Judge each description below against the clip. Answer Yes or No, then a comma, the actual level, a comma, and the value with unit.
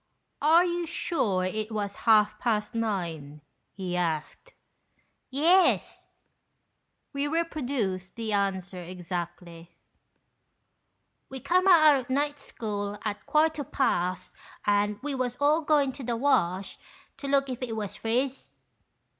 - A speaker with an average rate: No, slow, 120 wpm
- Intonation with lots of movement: Yes, wide, 7.0 semitones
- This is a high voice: Yes, high, 230 Hz